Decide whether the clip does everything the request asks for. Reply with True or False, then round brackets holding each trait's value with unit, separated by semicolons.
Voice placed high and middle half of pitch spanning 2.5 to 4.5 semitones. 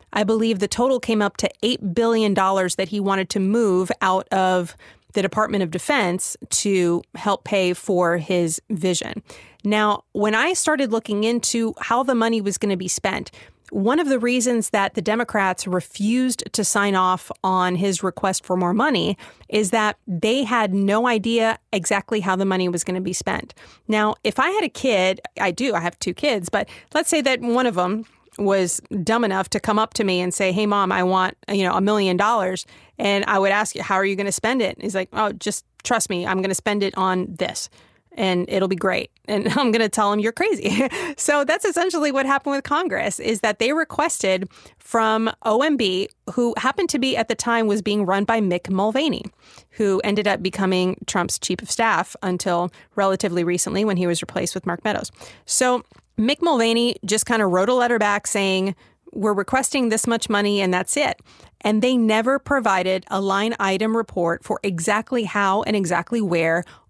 True (205 Hz; 3.4 semitones)